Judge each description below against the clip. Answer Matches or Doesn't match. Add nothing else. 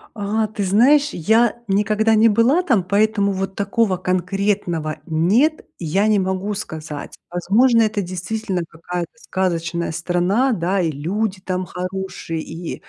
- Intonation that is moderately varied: Matches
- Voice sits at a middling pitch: Doesn't match